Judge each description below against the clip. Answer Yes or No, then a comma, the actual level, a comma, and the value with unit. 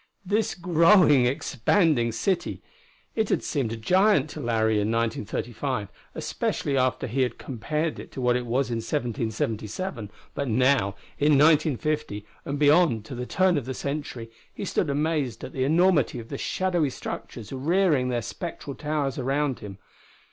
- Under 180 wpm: Yes, average, 155 wpm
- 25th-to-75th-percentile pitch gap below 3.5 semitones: No, average, 4.9 semitones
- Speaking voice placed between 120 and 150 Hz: Yes, low, 135 Hz